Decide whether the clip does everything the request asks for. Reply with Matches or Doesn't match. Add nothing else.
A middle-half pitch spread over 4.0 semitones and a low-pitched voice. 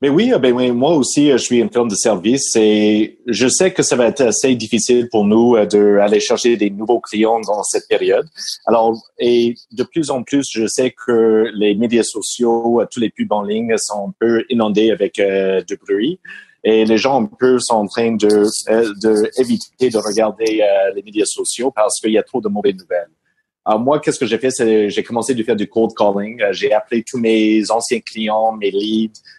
Doesn't match